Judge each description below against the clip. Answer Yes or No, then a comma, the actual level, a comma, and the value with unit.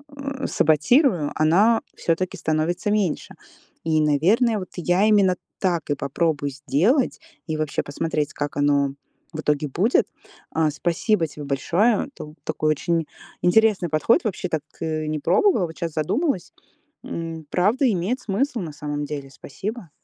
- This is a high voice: No, medium, 165 Hz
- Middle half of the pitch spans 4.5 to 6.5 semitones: Yes, wide, 5.5 semitones